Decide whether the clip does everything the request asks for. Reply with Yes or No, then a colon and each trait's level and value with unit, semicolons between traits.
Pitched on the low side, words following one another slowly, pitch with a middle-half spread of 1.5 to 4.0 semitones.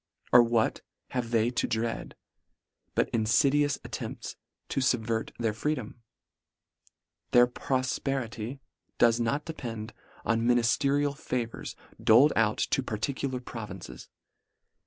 Yes: low, 120 Hz; slow, 105 wpm; average, 3.1 semitones